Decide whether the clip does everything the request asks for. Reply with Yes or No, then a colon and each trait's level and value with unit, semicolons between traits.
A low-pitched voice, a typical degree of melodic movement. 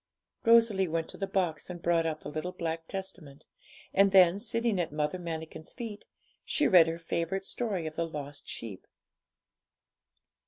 No: medium, 170 Hz; average, 3.3 semitones